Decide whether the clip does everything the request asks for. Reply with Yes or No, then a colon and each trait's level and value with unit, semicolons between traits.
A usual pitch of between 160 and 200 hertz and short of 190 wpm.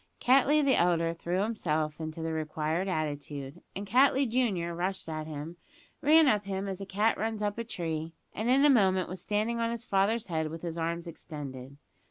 No: medium, 185 Hz; average, 195 wpm